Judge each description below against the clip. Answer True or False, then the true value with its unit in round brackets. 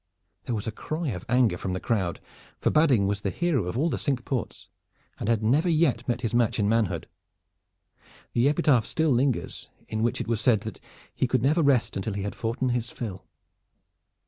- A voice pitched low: True (120 Hz)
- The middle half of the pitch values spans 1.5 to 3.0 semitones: False (4.2 semitones)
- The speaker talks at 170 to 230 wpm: True (200 wpm)